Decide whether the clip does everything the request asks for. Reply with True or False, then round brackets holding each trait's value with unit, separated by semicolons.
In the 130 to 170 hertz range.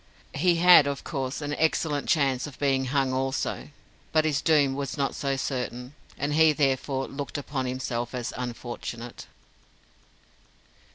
True (135 Hz)